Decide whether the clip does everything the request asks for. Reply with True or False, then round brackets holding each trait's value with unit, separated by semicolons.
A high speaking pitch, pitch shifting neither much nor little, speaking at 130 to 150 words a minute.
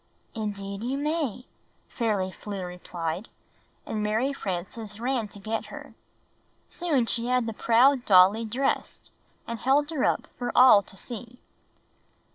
True (225 Hz; 4.0 semitones; 135 wpm)